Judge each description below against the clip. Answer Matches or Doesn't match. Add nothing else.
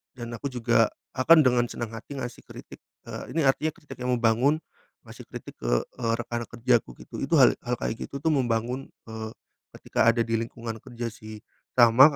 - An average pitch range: Doesn't match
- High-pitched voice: Doesn't match